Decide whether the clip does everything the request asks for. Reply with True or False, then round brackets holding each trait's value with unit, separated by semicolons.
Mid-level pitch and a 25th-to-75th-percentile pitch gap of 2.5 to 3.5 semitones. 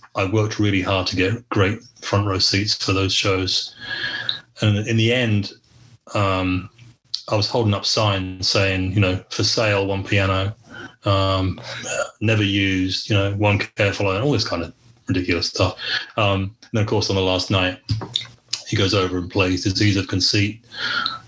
False (100 Hz; 2.8 semitones)